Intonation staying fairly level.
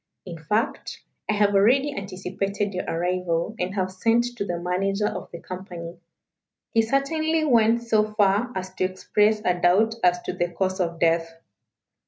No: average, 3.4 semitones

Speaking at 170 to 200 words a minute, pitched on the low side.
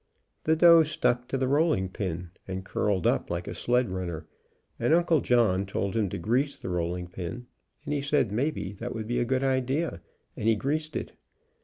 Yes: average, 195 wpm; low, 120 Hz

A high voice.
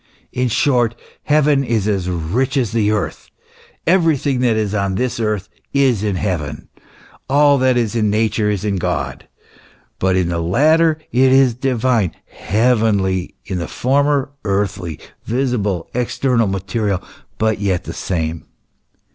No: low, 110 Hz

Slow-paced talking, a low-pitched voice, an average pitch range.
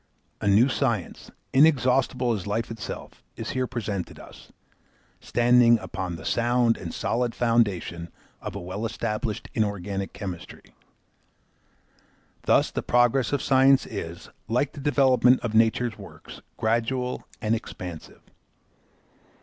Yes: slow, 120 wpm; low, 115 Hz; average, 3.6 semitones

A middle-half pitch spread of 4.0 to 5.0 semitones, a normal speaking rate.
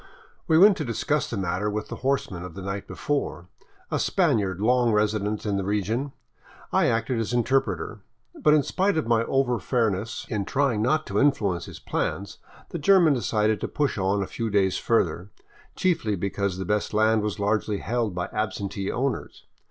Yes: average, 4.3 semitones; average, 180 wpm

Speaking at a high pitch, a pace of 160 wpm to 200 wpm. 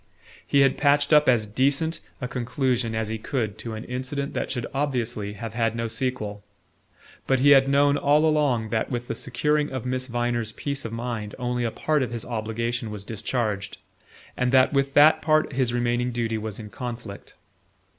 No: low, 120 Hz; average, 185 wpm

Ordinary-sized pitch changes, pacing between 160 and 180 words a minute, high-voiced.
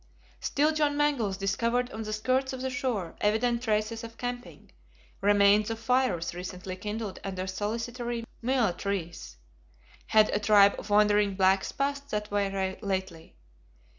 No: average, 3.8 semitones; average, 140 wpm; high, 215 Hz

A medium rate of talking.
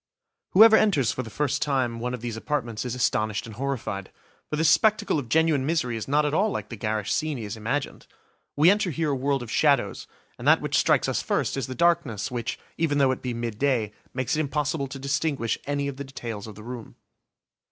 No: fast, 220 wpm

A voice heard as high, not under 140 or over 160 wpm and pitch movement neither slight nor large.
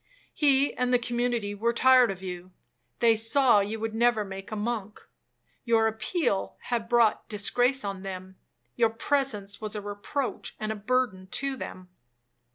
Yes: high, 225 Hz; average, 155 wpm; average, 3.3 semitones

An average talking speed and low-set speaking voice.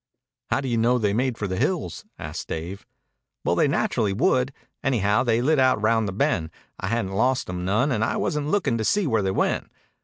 No: fast, 215 wpm; low, 115 Hz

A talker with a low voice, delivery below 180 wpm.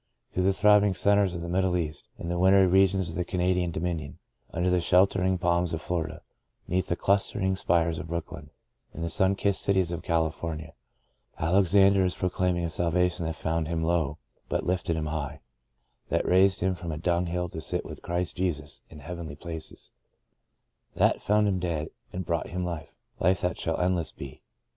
No: very low, 90 Hz; average, 190 wpm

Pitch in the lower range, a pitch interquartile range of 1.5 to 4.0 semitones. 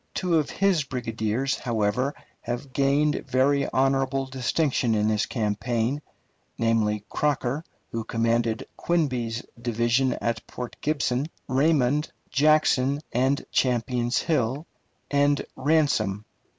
Yes: low, 130 Hz; average, 3.6 semitones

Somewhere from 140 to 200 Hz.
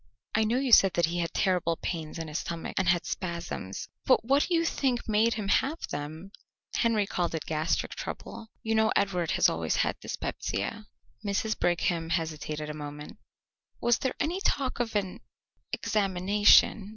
Yes: high, 190 Hz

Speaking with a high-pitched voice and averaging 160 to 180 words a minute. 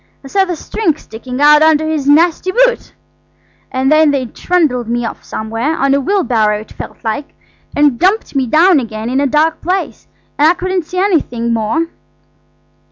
Yes: very high, 295 Hz; average, 170 wpm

